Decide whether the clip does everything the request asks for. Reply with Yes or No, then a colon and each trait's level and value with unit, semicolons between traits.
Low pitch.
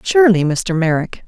No: high, 190 Hz